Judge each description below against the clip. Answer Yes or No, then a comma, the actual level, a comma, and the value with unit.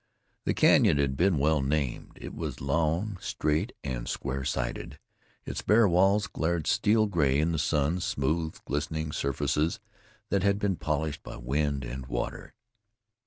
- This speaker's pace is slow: No, average, 150 wpm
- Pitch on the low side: Yes, very low, 75 Hz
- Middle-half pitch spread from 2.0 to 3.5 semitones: No, average, 3.9 semitones